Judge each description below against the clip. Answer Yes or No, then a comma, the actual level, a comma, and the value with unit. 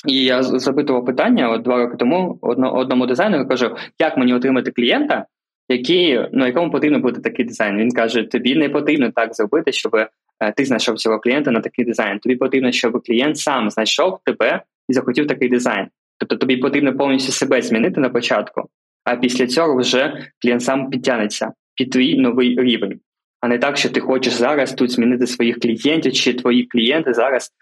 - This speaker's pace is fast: Yes, fast, 180 wpm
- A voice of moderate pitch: No, low, 125 Hz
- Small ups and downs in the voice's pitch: Yes, narrow, 1.5 semitones